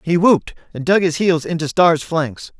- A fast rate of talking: Yes, fast, 210 wpm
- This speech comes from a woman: No, male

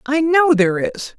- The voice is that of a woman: Yes, female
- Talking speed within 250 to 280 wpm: No, average, 200 wpm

